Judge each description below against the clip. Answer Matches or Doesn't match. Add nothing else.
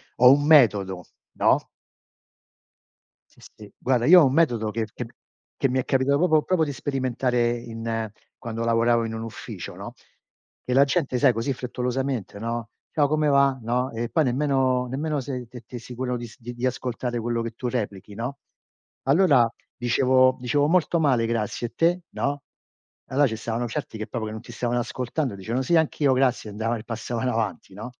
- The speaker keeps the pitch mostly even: Doesn't match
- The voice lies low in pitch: Matches